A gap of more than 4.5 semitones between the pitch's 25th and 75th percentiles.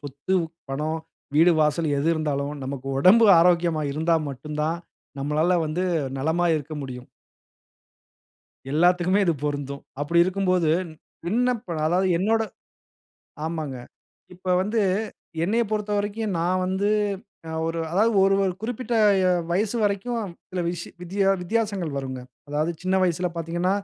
No: average, 4.2 semitones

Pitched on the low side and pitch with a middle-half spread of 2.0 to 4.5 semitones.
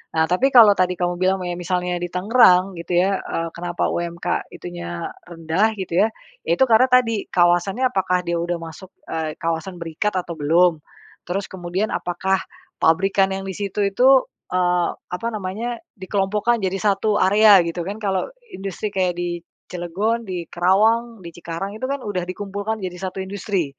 No: medium, 185 Hz; average, 2.8 semitones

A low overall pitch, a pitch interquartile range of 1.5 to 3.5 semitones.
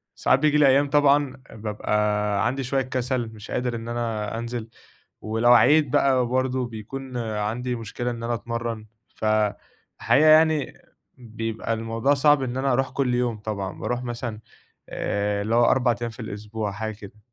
Yes: low, 120 Hz; average, 3.1 semitones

